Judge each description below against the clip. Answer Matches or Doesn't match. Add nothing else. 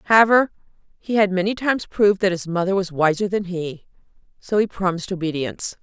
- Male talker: Doesn't match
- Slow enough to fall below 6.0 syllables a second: Doesn't match